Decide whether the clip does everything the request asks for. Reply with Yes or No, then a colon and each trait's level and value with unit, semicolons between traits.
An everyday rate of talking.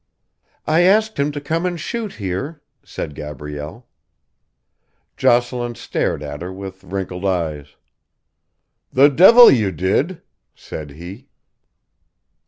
No: slow, 110 wpm